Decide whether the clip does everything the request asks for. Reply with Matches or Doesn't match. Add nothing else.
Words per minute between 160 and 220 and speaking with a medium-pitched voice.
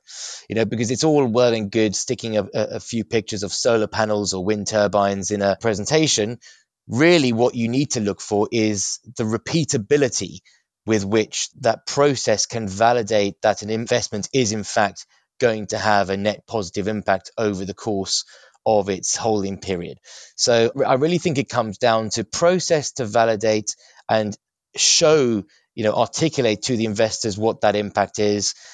Doesn't match